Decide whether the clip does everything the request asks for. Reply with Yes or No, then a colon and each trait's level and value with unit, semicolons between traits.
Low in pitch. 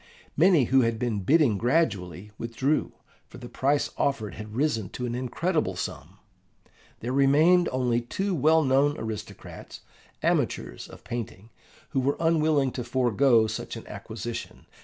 Yes: low, 130 Hz